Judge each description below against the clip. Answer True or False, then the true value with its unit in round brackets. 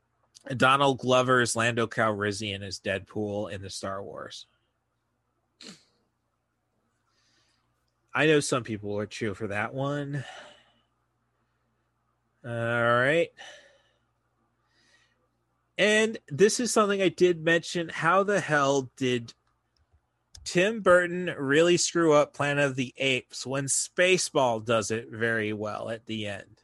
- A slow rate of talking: True (115 wpm)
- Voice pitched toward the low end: True (125 Hz)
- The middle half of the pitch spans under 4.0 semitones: False (5.0 semitones)